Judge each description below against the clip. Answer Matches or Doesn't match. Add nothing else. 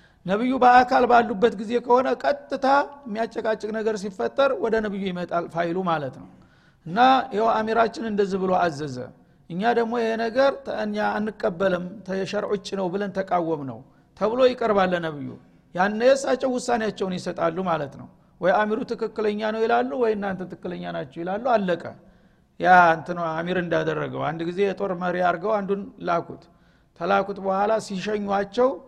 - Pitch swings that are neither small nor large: Matches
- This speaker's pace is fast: Matches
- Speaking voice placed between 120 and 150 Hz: Doesn't match